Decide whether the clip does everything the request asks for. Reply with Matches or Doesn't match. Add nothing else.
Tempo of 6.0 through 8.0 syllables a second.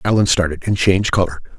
Matches